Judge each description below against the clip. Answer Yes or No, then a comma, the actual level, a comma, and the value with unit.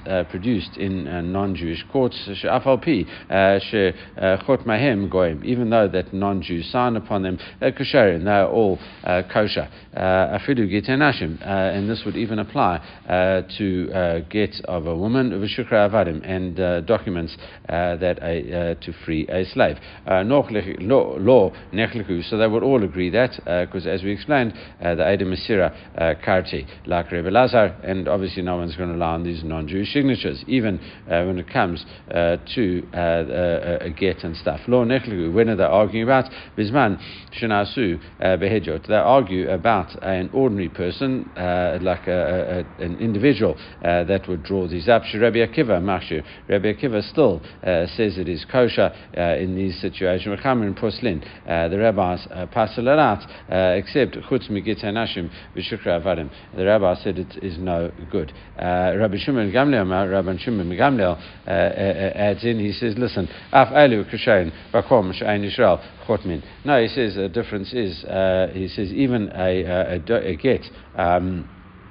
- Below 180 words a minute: Yes, average, 150 wpm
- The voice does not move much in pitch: No, average, 3.7 semitones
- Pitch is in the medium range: No, very low, 95 Hz